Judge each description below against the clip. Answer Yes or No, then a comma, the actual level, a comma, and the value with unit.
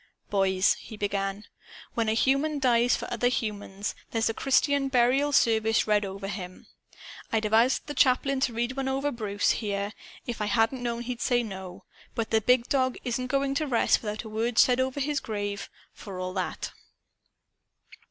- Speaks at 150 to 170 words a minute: No, average, 180 wpm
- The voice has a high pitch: Yes, high, 230 Hz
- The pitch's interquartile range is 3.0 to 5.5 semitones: Yes, average, 3.9 semitones